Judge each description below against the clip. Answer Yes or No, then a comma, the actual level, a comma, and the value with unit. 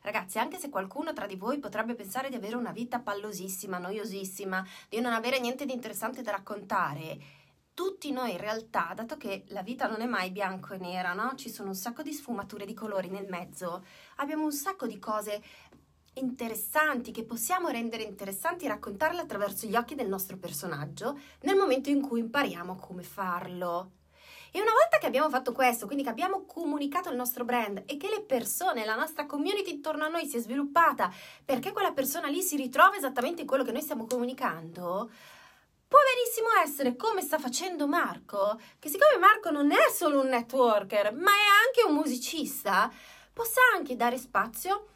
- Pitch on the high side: Yes, very high, 250 Hz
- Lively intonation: Yes, wide, 6.8 semitones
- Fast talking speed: Yes, fast, 185 wpm